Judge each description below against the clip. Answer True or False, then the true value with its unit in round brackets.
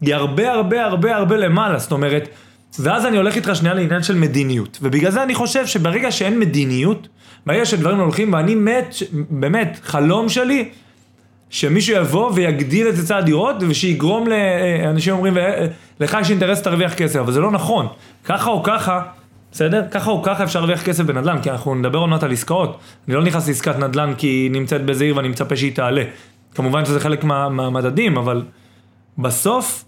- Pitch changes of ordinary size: False (6.3 semitones)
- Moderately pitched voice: True (165 Hz)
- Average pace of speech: False (160 wpm)